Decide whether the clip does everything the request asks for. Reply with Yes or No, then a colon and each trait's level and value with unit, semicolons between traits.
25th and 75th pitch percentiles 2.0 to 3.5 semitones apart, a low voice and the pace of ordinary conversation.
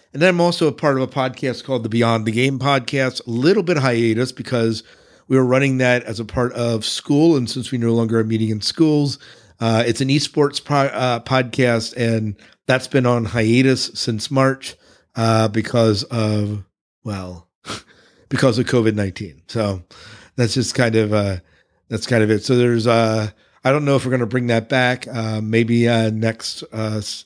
Yes: average, 2.8 semitones; low, 120 Hz; average, 190 wpm